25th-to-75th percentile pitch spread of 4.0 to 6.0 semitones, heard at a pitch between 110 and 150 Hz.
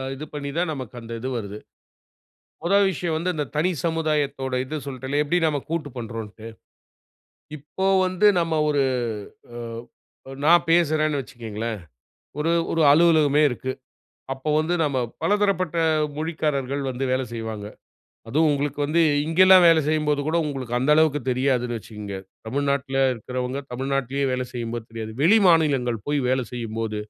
Yes: average, 4.3 semitones; medium, 140 Hz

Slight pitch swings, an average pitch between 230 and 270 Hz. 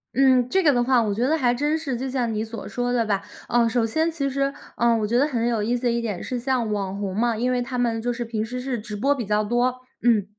Yes: narrow, 2.3 semitones; high, 240 Hz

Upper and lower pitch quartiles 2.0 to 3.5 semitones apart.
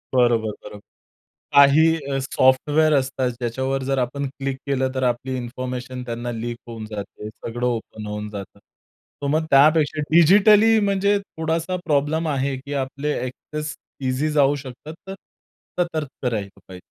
No: average, 4.0 semitones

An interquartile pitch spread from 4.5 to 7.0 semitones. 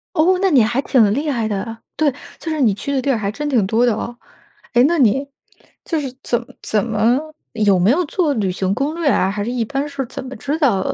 Yes: average, 4.9 semitones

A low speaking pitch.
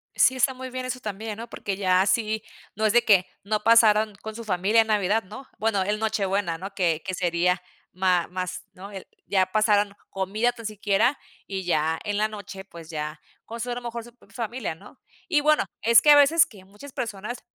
No: high, 210 Hz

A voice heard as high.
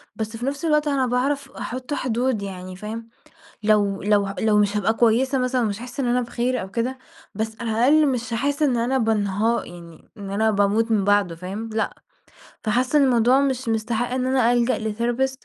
Yes: high, 230 Hz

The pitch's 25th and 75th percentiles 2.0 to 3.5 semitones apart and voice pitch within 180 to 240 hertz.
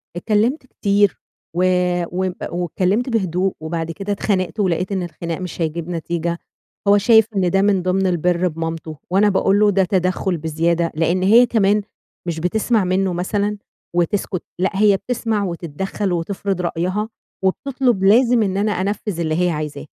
Yes: average, 3.2 semitones; medium, 185 Hz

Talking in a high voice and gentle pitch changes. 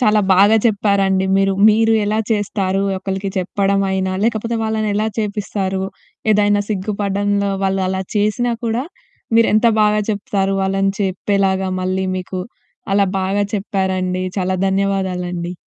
Yes: high, 195 Hz; narrow, 1.7 semitones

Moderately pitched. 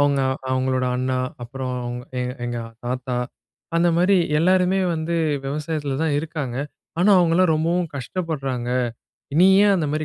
Yes: medium, 150 Hz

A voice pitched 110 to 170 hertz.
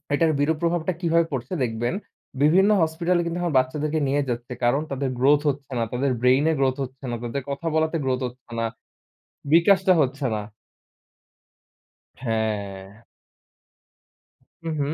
Yes: medium, 140 Hz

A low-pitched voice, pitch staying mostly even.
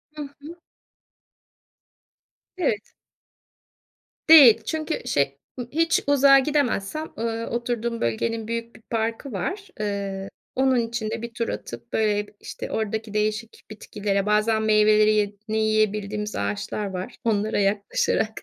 No: high, 220 Hz; narrow, 2.3 semitones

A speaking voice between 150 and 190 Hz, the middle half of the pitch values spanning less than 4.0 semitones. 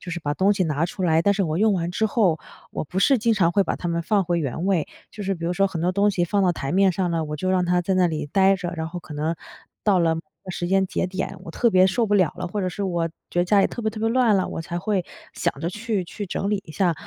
Yes: medium, 185 Hz; average, 2.8 semitones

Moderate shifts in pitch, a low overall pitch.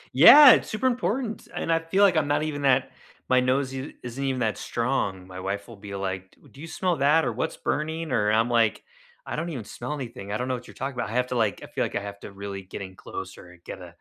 No: wide, 7.1 semitones; low, 125 Hz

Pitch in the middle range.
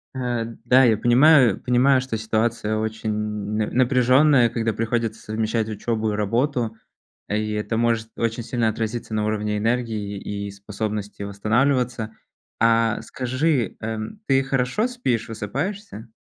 No: low, 115 Hz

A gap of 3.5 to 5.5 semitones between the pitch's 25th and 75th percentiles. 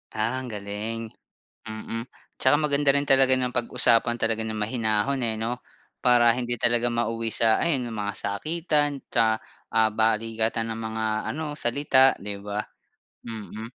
No: average, 2.7 semitones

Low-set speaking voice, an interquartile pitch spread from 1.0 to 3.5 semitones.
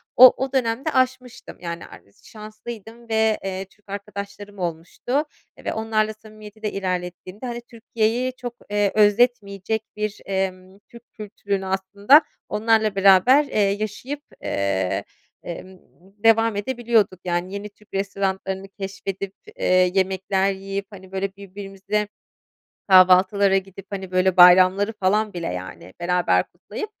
No: high, 200 Hz; narrow, 2.5 semitones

